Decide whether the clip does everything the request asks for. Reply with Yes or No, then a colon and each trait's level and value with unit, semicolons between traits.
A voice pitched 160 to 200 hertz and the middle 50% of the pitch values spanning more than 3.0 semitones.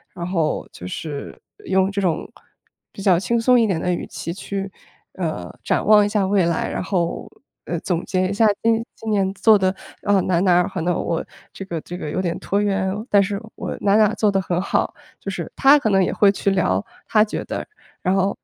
No: high, 190 Hz; narrow, 2.5 semitones